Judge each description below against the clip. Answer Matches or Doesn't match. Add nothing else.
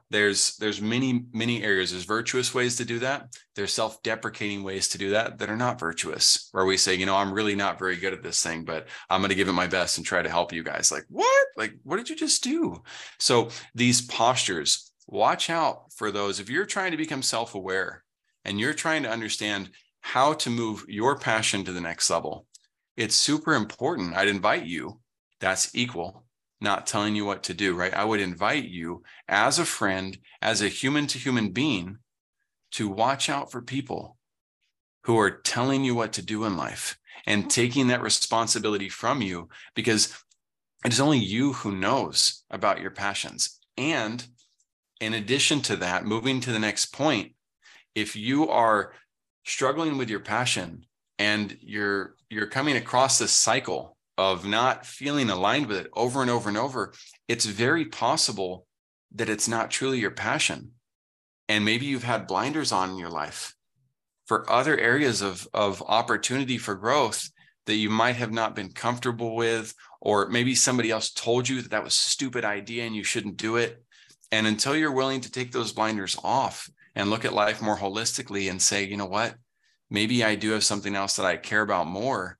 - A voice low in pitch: Matches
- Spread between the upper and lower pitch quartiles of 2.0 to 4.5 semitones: Matches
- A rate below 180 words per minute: Doesn't match